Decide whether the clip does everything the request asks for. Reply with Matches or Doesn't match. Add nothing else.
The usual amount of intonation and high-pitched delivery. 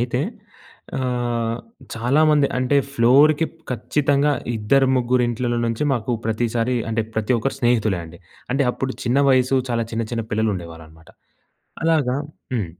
Doesn't match